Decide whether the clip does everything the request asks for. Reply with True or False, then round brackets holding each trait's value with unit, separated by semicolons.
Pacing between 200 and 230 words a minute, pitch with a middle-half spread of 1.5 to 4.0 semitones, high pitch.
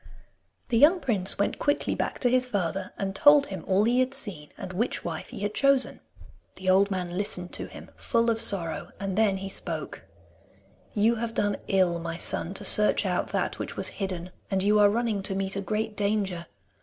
True (205 wpm; 3.3 semitones; 200 Hz)